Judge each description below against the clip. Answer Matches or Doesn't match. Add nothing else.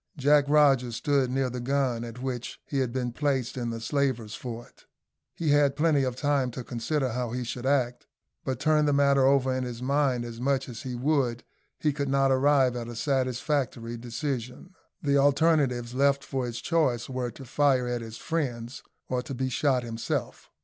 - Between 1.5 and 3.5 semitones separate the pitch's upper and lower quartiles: Matches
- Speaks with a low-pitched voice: Matches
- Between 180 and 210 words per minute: Matches